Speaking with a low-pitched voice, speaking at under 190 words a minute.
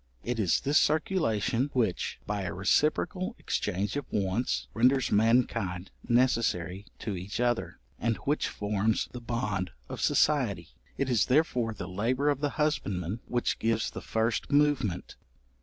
Yes: low, 115 Hz; average, 140 wpm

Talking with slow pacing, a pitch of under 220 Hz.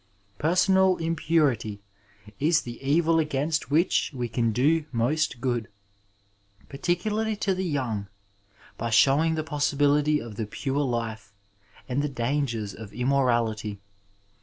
Yes: slow, 120 wpm; medium, 140 Hz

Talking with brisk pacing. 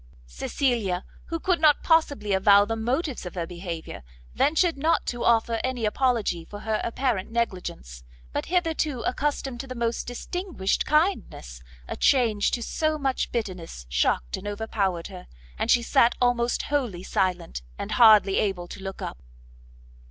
No: average, 150 wpm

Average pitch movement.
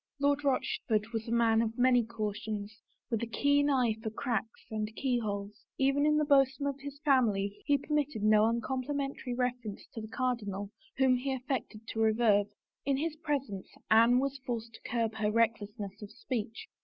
Yes: average, 3.9 semitones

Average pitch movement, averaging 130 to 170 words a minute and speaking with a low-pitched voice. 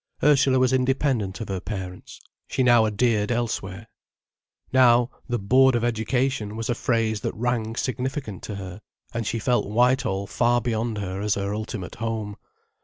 Yes: average, 3.2 semitones; average, 160 wpm; low, 115 Hz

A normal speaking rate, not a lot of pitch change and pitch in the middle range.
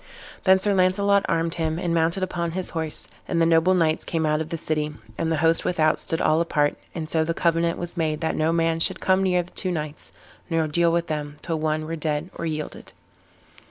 No: fast, 225 wpm; narrow, 1.8 semitones; medium, 165 Hz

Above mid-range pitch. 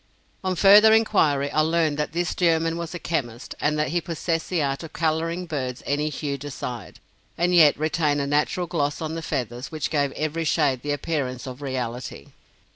No: medium, 155 Hz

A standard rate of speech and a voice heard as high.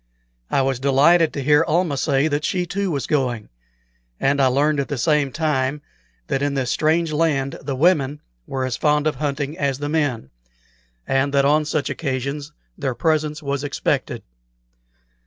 No: average, 170 wpm; medium, 145 Hz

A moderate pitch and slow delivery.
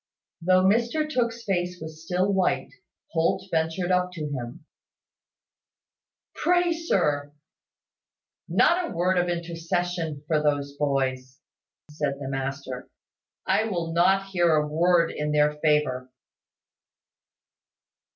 Yes: medium, 165 Hz; slow, 115 wpm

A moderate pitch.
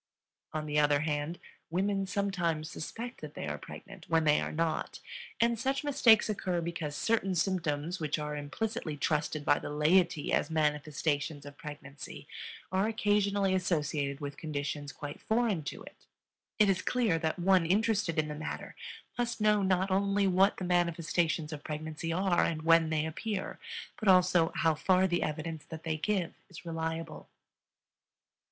Yes: medium, 165 Hz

